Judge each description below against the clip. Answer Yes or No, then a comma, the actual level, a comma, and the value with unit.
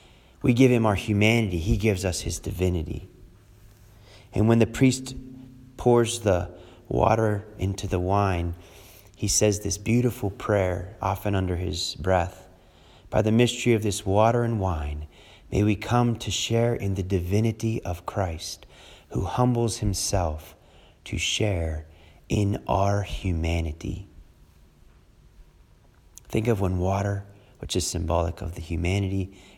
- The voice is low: Yes, low, 100 Hz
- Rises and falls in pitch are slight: No, average, 3.6 semitones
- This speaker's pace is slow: Yes, slow, 130 wpm